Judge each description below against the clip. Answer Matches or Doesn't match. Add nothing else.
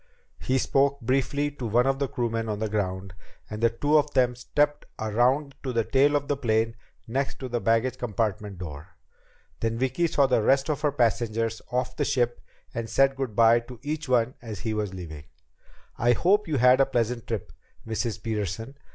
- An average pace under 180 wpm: Doesn't match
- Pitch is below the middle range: Matches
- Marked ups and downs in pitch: Doesn't match